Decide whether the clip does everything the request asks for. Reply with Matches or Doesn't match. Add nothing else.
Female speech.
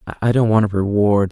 Doesn't match